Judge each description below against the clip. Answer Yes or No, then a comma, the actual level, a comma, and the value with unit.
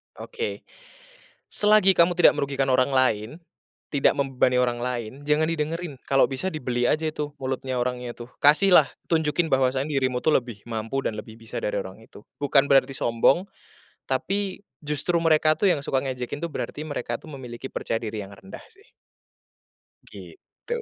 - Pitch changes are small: No, average, 4.1 semitones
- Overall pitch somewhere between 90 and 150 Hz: Yes, low, 135 Hz